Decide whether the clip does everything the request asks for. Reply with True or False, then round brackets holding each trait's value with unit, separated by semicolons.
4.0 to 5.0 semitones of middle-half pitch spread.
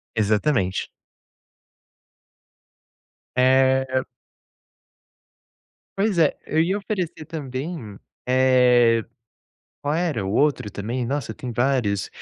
True (4.7 semitones)